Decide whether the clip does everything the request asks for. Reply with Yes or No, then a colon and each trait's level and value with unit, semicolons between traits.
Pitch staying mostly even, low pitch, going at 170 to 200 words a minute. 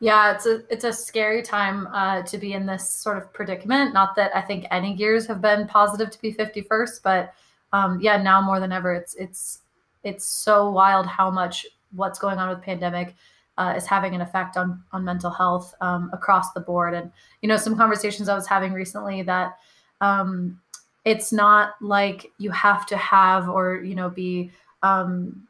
No: narrow, 2.1 semitones; high, 195 Hz; average, 195 wpm